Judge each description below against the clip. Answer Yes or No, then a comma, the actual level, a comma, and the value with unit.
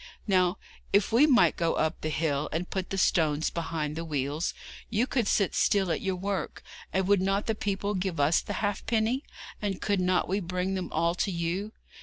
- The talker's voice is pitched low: No, medium, 185 Hz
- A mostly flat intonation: No, average, 3.5 semitones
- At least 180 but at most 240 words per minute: Yes, average, 200 wpm